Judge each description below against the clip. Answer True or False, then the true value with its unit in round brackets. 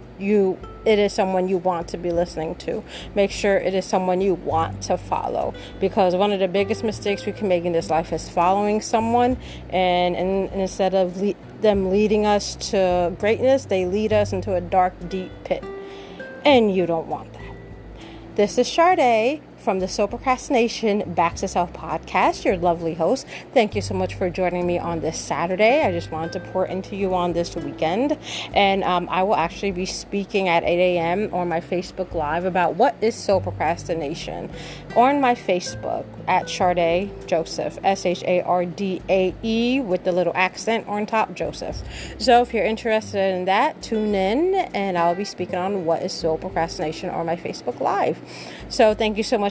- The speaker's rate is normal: True (180 wpm)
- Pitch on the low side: False (185 Hz)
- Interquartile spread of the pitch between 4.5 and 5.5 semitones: False (3.1 semitones)